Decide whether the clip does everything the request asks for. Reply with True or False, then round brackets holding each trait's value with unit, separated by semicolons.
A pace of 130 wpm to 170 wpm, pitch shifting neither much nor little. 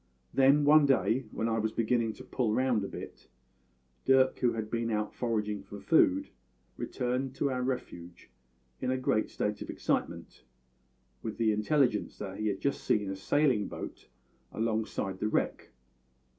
True (160 wpm; 3.7 semitones)